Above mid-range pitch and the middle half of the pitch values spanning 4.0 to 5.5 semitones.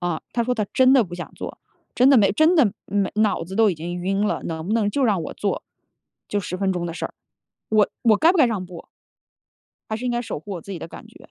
Yes: high, 205 Hz; average, 4.8 semitones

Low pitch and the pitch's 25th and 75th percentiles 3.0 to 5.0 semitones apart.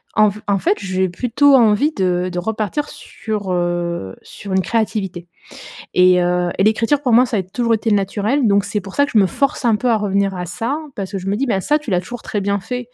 No: high, 205 Hz; average, 3.9 semitones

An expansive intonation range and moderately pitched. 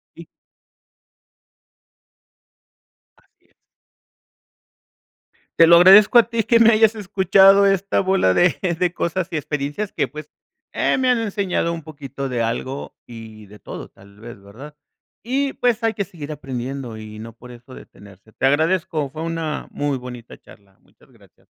Yes: wide, 7.9 semitones; medium, 155 Hz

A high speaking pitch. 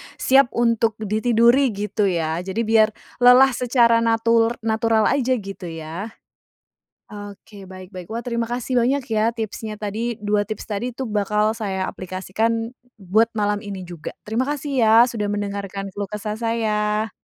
Yes: high, 220 Hz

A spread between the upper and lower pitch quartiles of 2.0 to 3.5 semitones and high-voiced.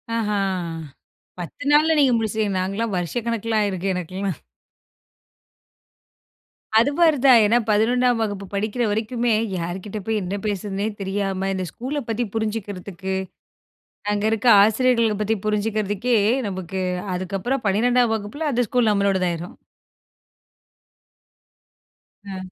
Yes: average, 3.2 semitones; high, 210 Hz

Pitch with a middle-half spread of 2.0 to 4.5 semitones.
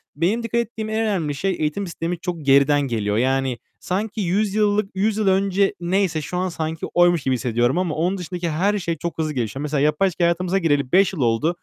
No: average, 4.9 semitones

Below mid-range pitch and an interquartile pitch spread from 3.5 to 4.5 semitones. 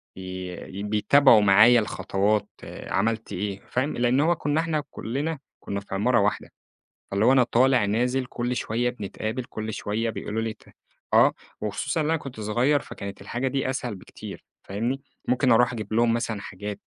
Yes: low, 115 Hz; average, 3.8 semitones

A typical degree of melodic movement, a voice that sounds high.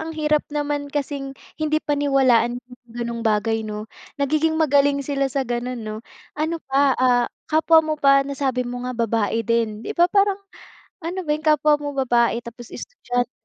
Yes: average, 3.8 semitones; very high, 275 Hz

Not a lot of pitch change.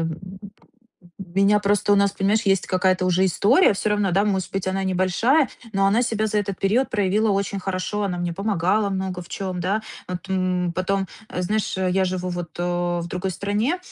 Yes: narrow, 2.0 semitones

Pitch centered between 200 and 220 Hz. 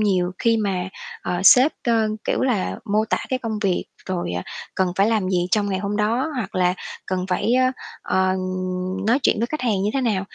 Yes: high, 210 Hz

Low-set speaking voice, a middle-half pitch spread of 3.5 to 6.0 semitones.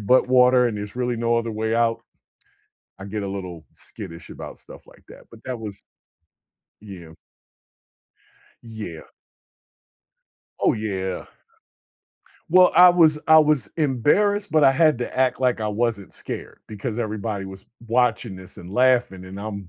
Yes: low, 115 Hz; average, 4.2 semitones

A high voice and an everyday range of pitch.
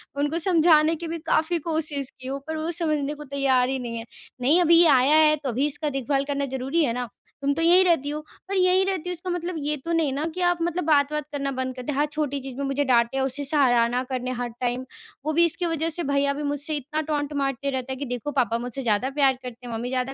Yes: very high, 285 Hz; average, 3.4 semitones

